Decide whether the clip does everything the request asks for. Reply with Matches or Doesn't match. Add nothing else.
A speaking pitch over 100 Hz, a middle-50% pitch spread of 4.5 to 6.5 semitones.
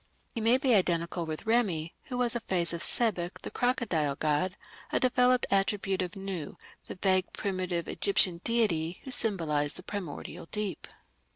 Matches